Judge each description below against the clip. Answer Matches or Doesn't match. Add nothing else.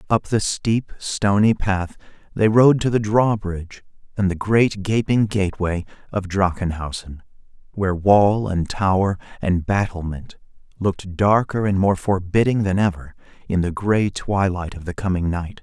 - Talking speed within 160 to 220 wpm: Doesn't match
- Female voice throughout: Doesn't match